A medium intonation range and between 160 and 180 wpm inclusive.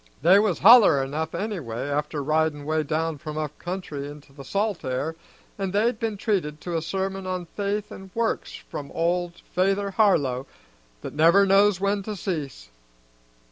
Yes: average, 4.9 semitones; average, 165 wpm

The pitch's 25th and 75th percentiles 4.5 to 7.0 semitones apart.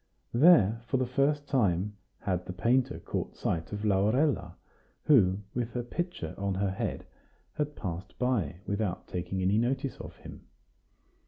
Yes: wide, 5.6 semitones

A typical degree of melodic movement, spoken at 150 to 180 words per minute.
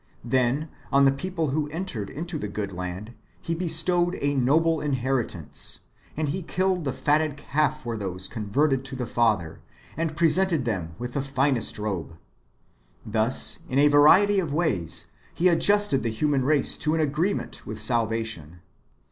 No: wide, 6.2 semitones; average, 165 wpm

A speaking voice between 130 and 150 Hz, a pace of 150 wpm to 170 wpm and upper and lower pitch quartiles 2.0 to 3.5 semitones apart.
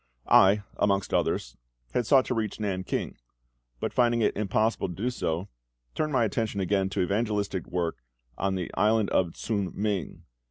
No: low, 100 Hz; average, 165 wpm; average, 2.9 semitones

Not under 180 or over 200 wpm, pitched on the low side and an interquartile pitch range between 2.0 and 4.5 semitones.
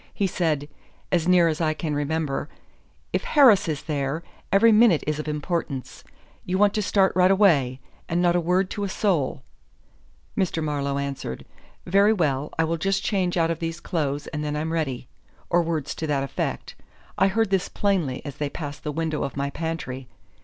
No: average, 190 wpm; medium, 160 Hz; average, 4.0 semitones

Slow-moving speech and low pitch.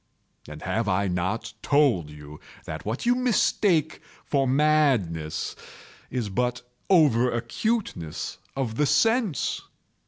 Yes: slow, 115 wpm; low, 125 Hz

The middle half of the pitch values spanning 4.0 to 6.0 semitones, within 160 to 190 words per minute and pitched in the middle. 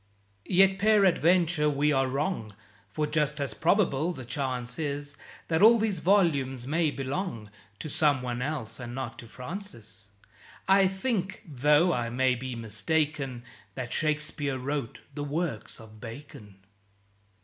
No: average, 5.1 semitones; slow, 135 wpm; medium, 145 Hz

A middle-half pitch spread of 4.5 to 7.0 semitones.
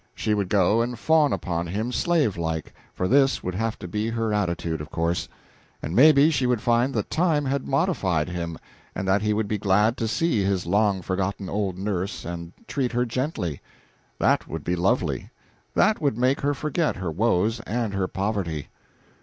Yes: wide, 5.5 semitones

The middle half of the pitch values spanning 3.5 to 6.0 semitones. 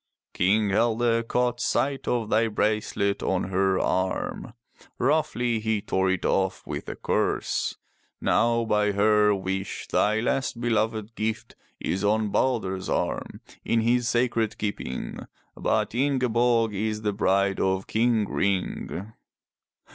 No: average, 2.9 semitones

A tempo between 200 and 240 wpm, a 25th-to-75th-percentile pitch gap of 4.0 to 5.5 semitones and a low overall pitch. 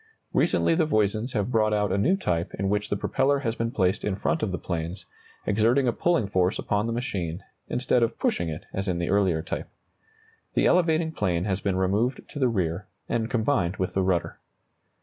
Yes: fast, 205 wpm; average, 4.8 semitones; low, 105 Hz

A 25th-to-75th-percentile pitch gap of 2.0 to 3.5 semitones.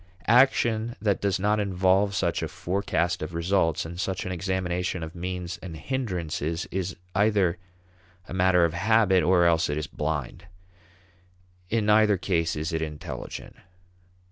Yes: average, 3.1 semitones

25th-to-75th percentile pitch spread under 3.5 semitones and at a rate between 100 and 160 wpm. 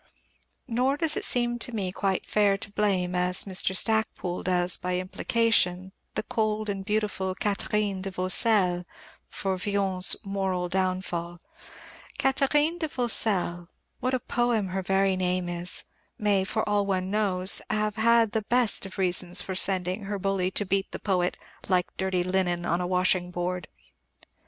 Yes: average, 2.7 semitones; average, 155 wpm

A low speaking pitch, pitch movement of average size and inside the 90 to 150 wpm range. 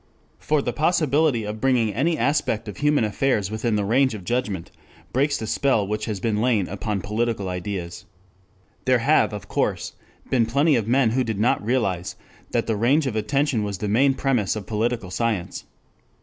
No: low, 115 Hz; average, 4.2 semitones; average, 175 wpm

